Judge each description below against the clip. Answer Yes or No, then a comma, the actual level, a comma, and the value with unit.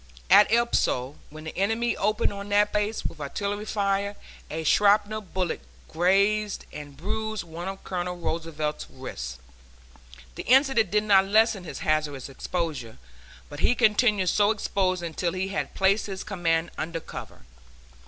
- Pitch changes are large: No, average, 4.3 semitones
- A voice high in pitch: Yes, high, 195 Hz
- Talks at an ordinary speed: Yes, average, 150 wpm